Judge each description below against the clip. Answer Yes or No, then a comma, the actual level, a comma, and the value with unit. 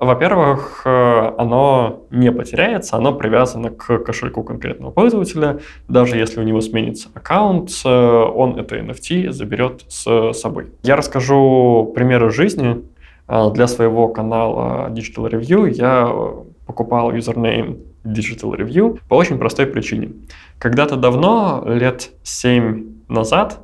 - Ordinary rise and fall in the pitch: Yes, average, 3.2 semitones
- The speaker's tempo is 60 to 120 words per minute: Yes, average, 115 wpm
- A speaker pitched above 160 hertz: No, low, 120 Hz